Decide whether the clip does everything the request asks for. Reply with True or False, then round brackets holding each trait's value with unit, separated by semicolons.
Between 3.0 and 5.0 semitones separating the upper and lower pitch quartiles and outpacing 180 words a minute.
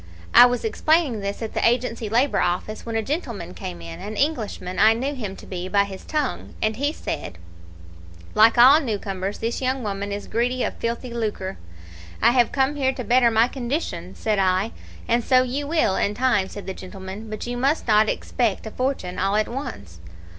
True (4.3 semitones; 200 wpm)